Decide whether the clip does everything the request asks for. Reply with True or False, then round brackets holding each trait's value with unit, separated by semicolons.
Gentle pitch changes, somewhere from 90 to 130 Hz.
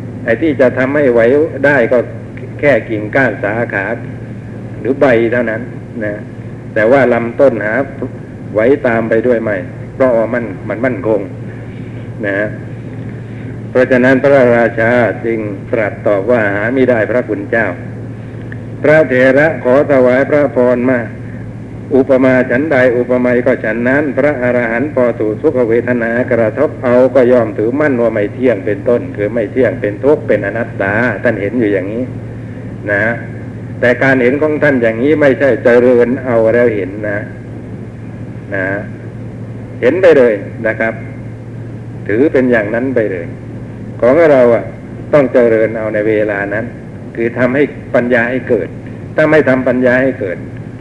True (1.8 semitones; 120 Hz)